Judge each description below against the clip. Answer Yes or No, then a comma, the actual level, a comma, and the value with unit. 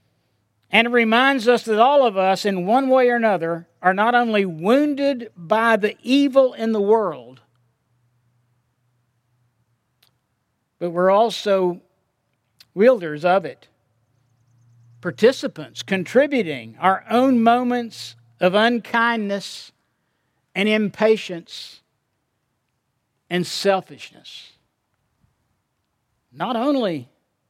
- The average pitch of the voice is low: No, medium, 180 Hz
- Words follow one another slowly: Yes, slow, 90 wpm